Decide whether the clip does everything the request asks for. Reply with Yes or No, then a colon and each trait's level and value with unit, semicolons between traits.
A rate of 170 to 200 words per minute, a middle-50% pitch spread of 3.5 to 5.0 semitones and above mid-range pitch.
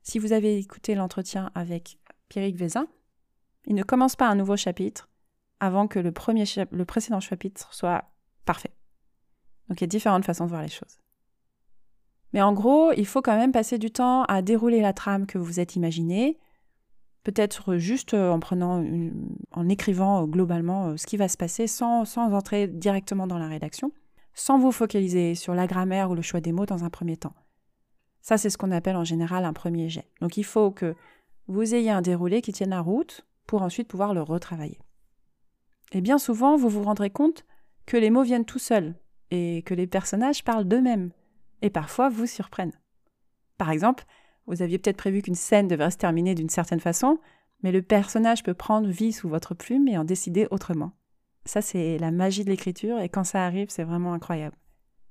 Yes: average, 195 wpm; average, 4.1 semitones; high, 195 Hz